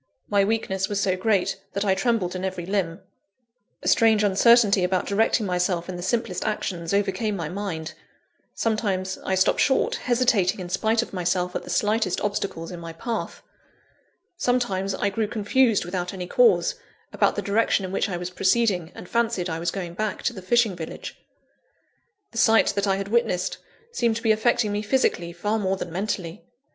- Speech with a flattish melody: No, average, 3.5 semitones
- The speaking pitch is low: No, high, 195 Hz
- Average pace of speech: Yes, average, 180 wpm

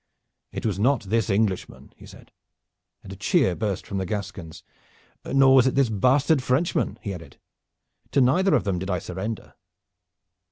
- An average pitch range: No, wide, 5.8 semitones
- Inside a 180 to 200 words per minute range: No, average, 165 wpm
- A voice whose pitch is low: Yes, low, 110 Hz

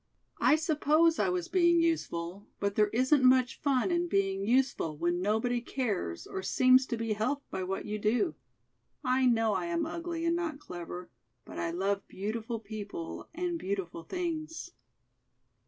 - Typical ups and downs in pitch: No, wide, 8.1 semitones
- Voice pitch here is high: Yes, high, 240 Hz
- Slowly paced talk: No, average, 160 wpm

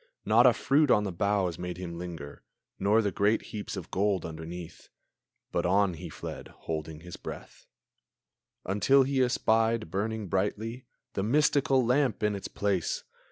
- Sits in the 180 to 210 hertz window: No, low, 100 Hz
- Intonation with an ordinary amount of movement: Yes, average, 4.3 semitones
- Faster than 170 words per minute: No, average, 155 wpm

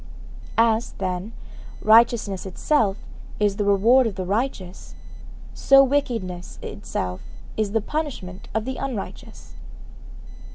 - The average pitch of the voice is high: Yes, high, 215 Hz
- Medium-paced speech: No, slow, 110 wpm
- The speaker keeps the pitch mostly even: No, average, 4.5 semitones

